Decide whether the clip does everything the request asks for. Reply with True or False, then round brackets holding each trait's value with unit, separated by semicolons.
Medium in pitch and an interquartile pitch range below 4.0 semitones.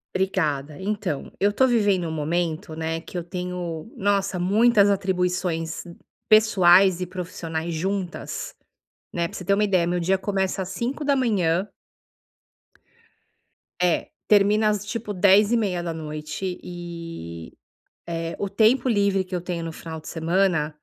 True (180 Hz; 3.3 semitones)